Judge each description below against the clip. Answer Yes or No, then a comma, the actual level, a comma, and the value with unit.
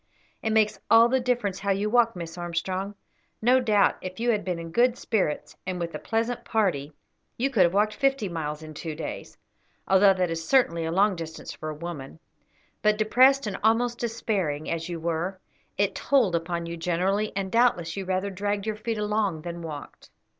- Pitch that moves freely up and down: No, average, 4.6 semitones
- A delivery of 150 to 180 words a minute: No, average, 195 wpm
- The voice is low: No, high, 195 Hz